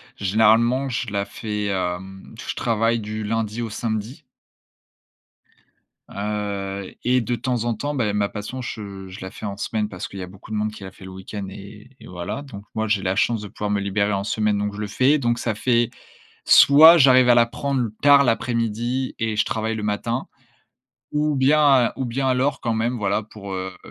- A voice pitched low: Yes, low, 110 Hz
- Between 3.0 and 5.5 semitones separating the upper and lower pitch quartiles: Yes, average, 3.3 semitones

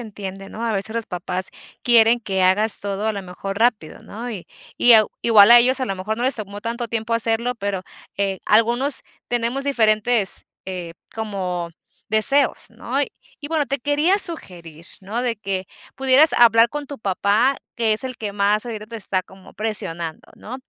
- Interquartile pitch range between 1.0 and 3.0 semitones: No, average, 3.5 semitones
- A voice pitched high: Yes, high, 220 Hz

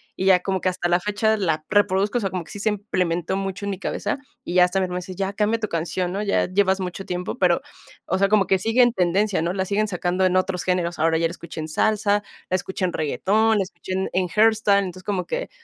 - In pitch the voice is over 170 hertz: Yes, high, 190 Hz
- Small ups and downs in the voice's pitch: Yes, narrow, 2.3 semitones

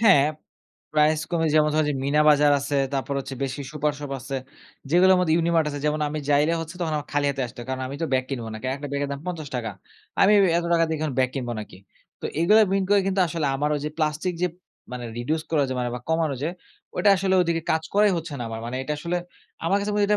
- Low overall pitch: No, medium, 150 Hz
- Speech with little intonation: No, average, 3.4 semitones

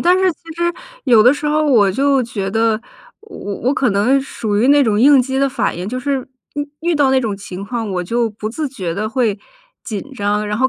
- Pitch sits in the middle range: No, high, 240 Hz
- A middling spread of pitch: Yes, average, 4.9 semitones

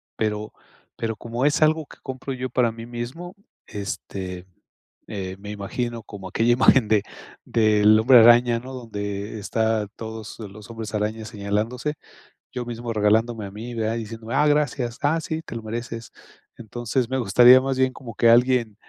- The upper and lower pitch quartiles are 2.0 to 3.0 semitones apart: Yes, average, 2.7 semitones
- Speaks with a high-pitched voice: No, low, 115 Hz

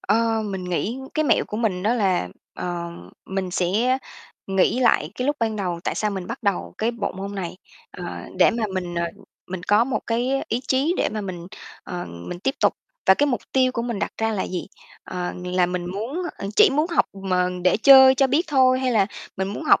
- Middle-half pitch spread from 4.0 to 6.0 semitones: Yes, wide, 5.5 semitones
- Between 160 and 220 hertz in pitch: Yes, high, 210 Hz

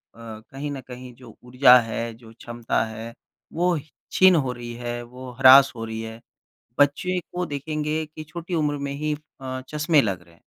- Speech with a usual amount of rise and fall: Yes, average, 4.6 semitones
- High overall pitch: No, low, 130 Hz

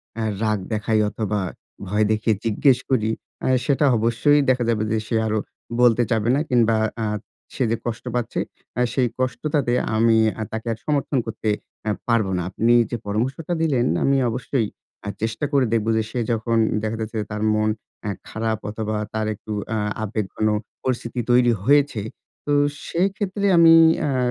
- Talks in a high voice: No, low, 115 Hz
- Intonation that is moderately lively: Yes, average, 3.1 semitones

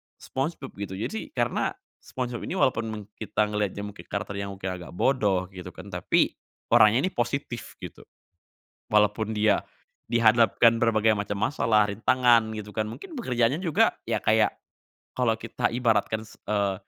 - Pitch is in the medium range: No, low, 110 Hz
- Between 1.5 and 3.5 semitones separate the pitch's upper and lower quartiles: Yes, average, 2.7 semitones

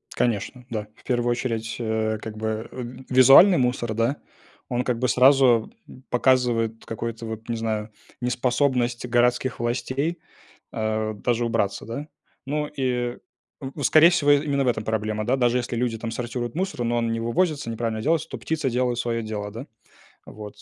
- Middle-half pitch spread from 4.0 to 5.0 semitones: No, narrow, 2.5 semitones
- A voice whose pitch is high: No, low, 120 Hz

